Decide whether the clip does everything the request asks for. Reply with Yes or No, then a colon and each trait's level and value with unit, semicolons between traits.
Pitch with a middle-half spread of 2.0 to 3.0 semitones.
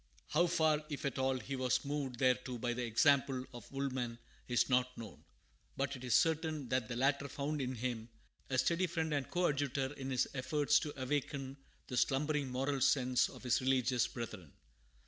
Yes: narrow, 2.5 semitones